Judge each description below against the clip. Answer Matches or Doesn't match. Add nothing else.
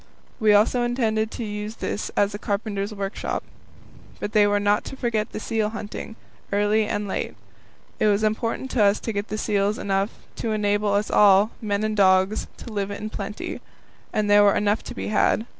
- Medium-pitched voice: Doesn't match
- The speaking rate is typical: Matches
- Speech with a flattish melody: Matches